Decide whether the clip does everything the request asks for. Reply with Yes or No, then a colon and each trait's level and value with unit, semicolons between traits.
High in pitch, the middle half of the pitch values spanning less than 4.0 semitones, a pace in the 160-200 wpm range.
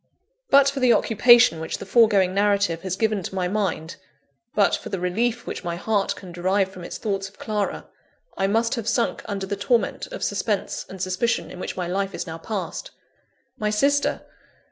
Yes: high, 200 Hz; average, 3.3 semitones; average, 190 wpm